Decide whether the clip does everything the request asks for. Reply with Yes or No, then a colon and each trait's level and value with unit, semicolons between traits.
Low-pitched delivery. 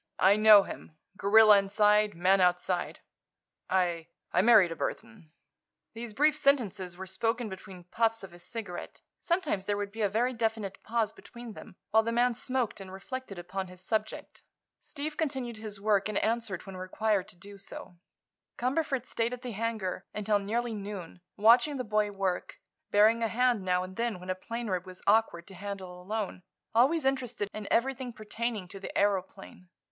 No: high, 210 Hz